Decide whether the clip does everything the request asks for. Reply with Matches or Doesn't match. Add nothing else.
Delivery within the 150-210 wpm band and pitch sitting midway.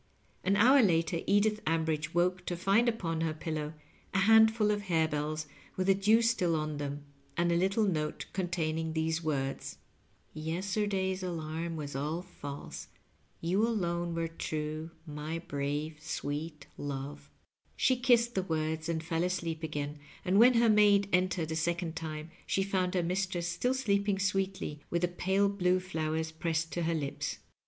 Matches